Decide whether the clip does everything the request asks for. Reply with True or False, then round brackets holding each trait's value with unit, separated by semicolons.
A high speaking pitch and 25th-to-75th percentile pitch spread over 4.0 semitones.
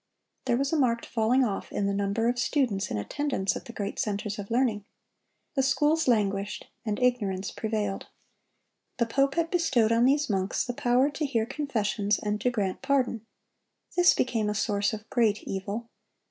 True (230 Hz; 4.4 semitones)